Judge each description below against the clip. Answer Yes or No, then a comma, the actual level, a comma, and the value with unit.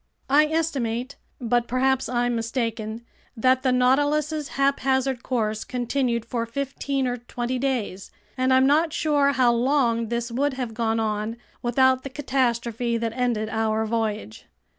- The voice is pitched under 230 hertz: No, high, 245 Hz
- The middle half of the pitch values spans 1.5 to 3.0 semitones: Yes, narrow, 2.6 semitones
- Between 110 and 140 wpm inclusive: Yes, slow, 135 wpm